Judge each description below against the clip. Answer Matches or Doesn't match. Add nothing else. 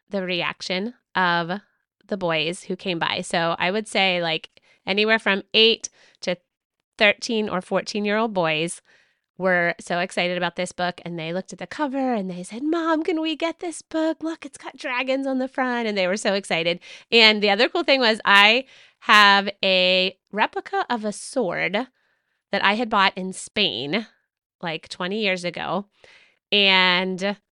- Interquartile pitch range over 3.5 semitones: Matches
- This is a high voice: Matches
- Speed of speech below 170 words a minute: Doesn't match